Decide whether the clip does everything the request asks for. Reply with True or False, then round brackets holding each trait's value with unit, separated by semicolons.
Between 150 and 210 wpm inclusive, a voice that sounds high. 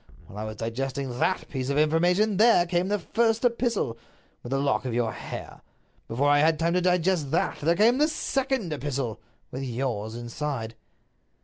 False (180 wpm; 150 Hz)